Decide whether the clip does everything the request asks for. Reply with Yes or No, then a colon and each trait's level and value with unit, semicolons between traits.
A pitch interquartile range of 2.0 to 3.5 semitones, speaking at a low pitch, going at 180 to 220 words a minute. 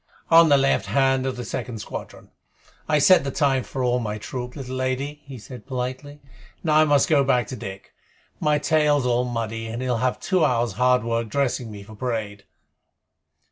Yes: average, 3.1 semitones; low, 130 Hz; average, 190 wpm